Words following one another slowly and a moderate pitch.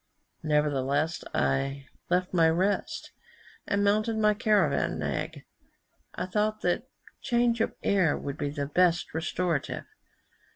Yes: slow, 120 wpm; medium, 180 Hz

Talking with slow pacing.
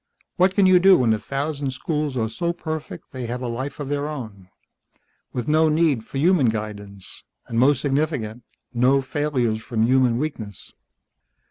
No: average, 165 wpm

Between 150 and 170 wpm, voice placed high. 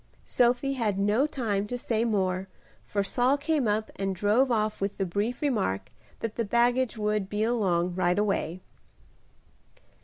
Yes: average, 155 wpm; high, 210 Hz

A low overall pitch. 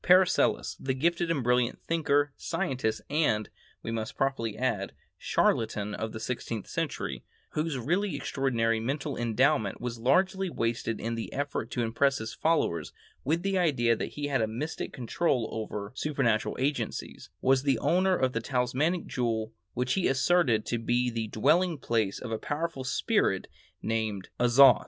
Yes: low, 125 Hz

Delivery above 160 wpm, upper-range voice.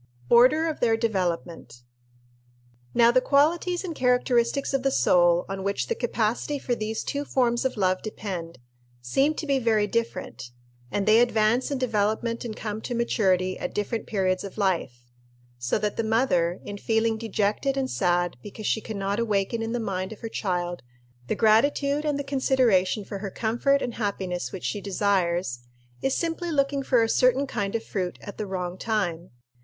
Yes: average, 180 wpm; high, 220 Hz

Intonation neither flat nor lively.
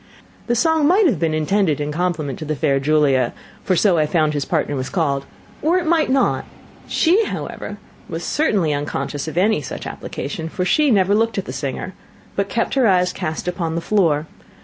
No: wide, 6.4 semitones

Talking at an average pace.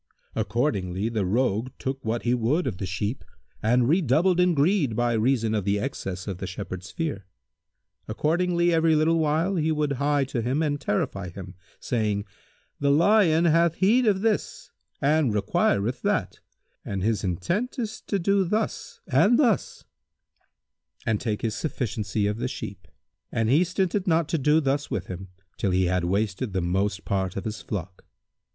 Yes: average, 170 wpm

